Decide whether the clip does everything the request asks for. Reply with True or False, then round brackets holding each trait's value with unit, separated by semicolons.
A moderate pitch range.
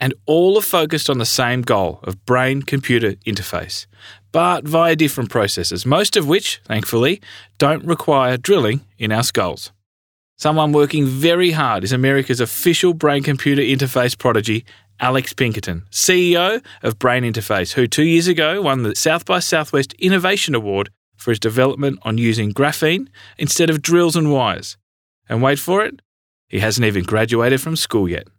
False (6.3 semitones)